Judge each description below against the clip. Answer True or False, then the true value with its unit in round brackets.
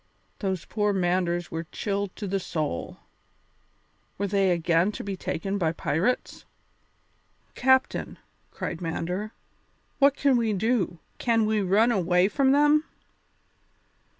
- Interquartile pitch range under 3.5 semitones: False (4.2 semitones)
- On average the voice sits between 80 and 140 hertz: False (195 Hz)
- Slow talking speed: True (125 wpm)